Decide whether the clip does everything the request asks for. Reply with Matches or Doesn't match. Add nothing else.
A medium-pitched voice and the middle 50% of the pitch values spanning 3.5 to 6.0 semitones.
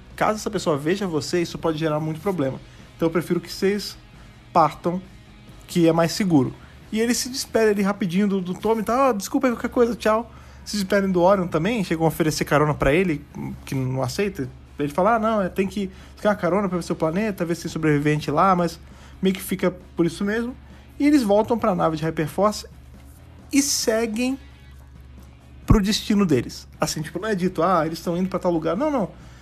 Matches